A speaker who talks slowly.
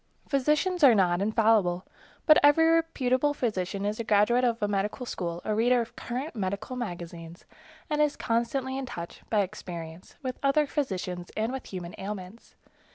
No: average, 160 wpm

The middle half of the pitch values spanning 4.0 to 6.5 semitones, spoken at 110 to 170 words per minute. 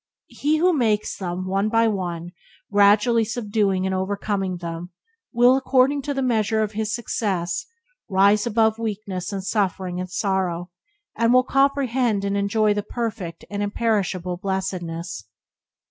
No: average, 3.5 semitones; average, 140 wpm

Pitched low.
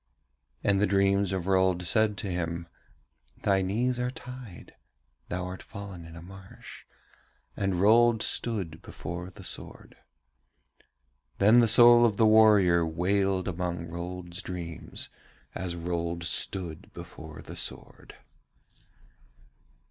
Yes: very low, 95 Hz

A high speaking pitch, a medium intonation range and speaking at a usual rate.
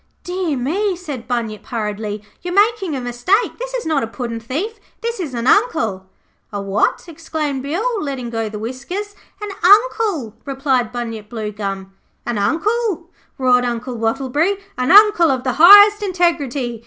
No: very high, 275 Hz; wide, 8.2 semitones; average, 155 wpm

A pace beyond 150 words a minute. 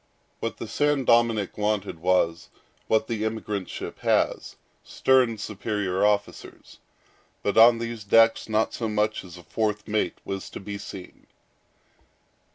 No: average, 140 wpm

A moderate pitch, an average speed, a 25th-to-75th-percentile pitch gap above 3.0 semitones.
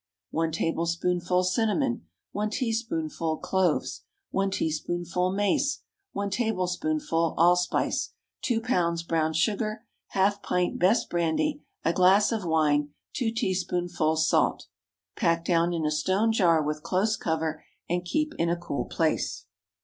No: medium, 180 Hz; slow, 125 wpm; average, 4.0 semitones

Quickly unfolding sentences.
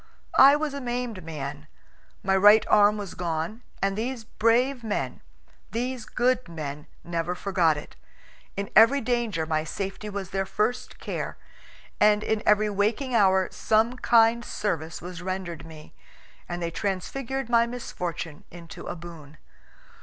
No: average, 145 wpm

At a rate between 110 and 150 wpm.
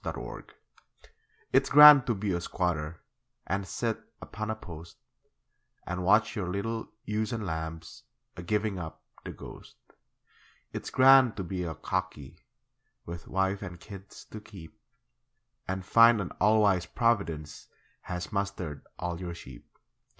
Yes: average, 145 wpm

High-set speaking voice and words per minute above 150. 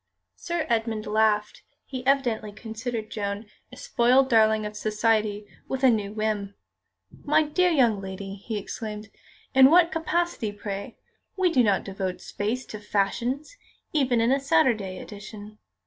No: high, 220 Hz; average, 145 wpm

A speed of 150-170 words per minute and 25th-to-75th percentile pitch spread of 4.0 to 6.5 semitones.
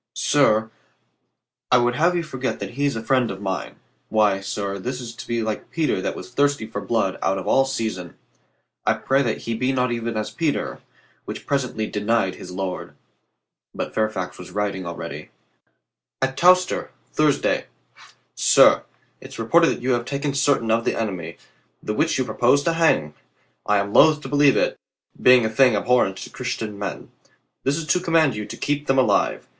No: average, 185 wpm; average, 4.9 semitones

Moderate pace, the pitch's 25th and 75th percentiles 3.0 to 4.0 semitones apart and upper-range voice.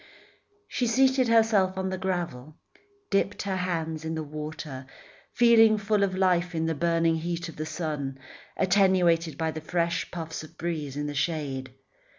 No: average, 165 wpm; average, 3.3 semitones; medium, 170 Hz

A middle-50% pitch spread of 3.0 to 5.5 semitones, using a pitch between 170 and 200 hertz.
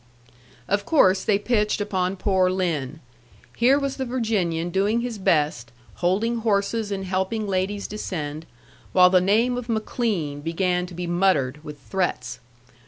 Yes: average, 3.8 semitones; high, 190 Hz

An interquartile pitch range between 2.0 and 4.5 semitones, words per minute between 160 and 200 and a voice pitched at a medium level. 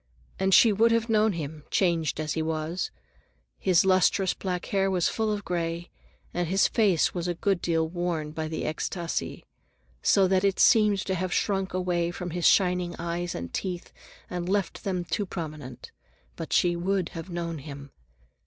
Yes: narrow, 2.5 semitones; average, 175 wpm; medium, 175 Hz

